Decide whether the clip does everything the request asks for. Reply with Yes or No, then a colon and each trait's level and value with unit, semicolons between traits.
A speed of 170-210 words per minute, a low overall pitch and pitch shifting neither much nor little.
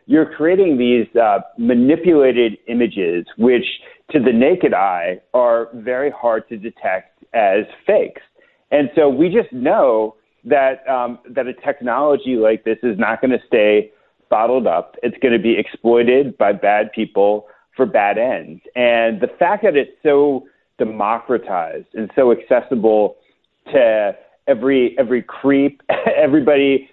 No: average, 140 wpm; low, 120 Hz; average, 3.8 semitones